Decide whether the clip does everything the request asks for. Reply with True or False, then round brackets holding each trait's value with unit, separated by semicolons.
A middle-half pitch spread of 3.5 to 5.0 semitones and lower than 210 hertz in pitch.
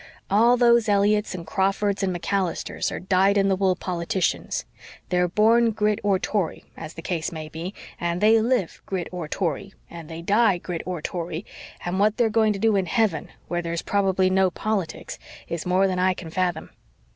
False (3.1 semitones; 190 Hz)